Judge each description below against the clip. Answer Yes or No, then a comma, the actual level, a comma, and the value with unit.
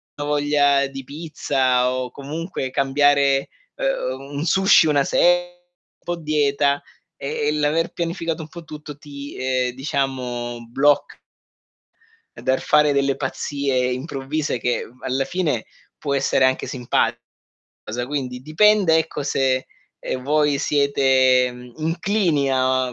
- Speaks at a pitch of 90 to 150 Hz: Yes, medium, 140 Hz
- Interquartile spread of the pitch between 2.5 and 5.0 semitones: Yes, average, 2.8 semitones